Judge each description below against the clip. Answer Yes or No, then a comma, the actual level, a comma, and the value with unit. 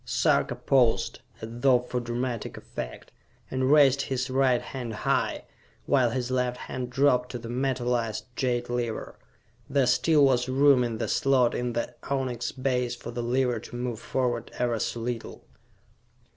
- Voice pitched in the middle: No, low, 125 Hz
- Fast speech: No, average, 160 wpm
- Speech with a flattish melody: Yes, narrow, 1.6 semitones